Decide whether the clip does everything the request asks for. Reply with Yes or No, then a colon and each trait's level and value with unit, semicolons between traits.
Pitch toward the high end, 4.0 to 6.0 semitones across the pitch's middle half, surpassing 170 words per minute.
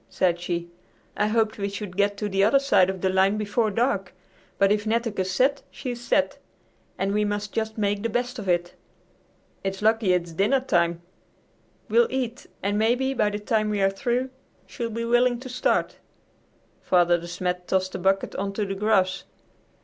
No: high, 205 Hz; average, 3.4 semitones; average, 185 wpm